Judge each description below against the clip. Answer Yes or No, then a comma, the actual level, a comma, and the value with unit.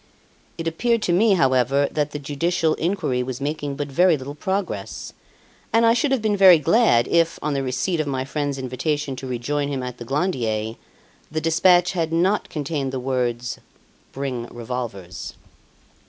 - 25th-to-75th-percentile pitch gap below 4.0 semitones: No, average, 4.8 semitones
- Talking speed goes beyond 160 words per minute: Yes, average, 170 wpm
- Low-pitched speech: No, medium, 145 Hz